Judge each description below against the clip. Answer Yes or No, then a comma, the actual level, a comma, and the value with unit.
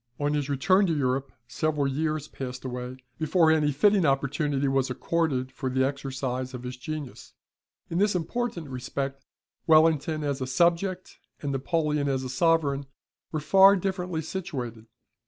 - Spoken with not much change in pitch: No, average, 3.8 semitones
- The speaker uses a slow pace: No, average, 150 wpm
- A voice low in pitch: No, medium, 145 Hz